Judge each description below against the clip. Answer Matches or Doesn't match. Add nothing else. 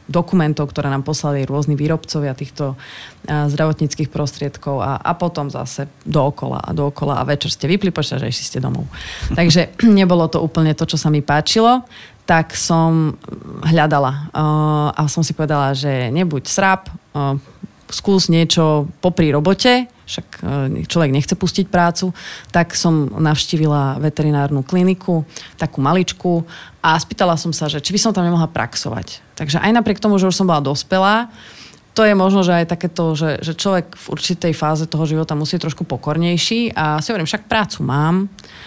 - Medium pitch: Matches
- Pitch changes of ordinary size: Matches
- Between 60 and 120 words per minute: Doesn't match